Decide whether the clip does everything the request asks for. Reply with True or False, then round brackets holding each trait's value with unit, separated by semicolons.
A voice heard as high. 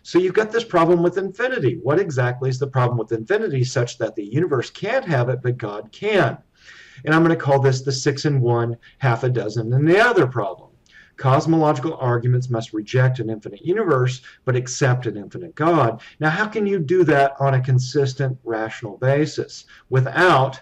False (130 Hz)